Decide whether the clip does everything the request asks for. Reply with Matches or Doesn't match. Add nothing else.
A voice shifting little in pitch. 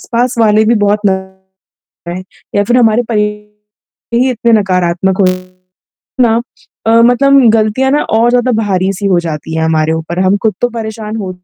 Doesn't match